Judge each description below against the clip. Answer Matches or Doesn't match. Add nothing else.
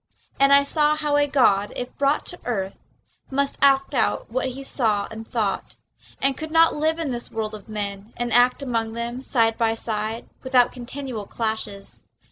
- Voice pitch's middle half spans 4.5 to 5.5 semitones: Doesn't match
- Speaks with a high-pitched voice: Matches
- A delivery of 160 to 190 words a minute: Matches